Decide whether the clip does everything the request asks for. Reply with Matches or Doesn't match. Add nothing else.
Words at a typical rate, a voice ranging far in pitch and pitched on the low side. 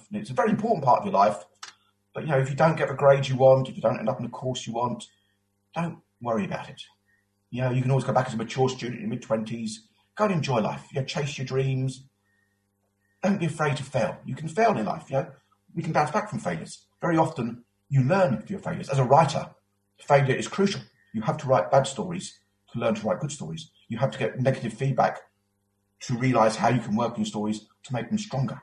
Doesn't match